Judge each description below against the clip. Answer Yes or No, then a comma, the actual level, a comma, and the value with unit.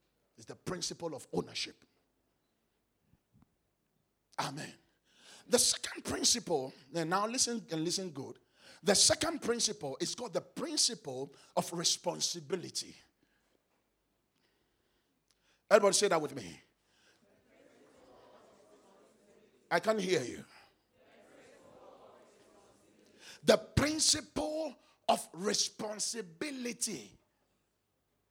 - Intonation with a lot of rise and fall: Yes, wide, 6.2 semitones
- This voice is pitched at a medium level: No, high, 205 Hz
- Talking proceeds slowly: Yes, slow, 80 wpm